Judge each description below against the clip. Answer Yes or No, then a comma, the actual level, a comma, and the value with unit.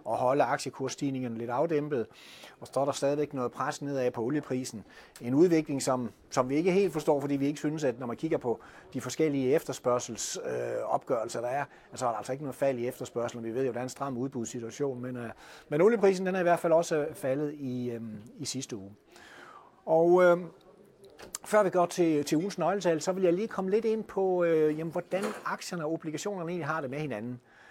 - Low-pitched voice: No, medium, 145 Hz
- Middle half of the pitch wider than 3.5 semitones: Yes, average, 4.8 semitones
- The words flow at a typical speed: Yes, average, 215 wpm